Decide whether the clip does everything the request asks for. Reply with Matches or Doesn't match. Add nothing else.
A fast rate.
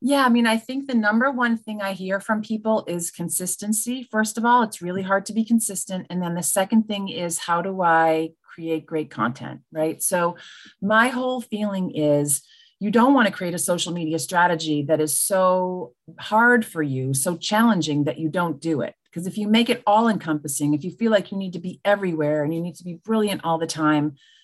Matches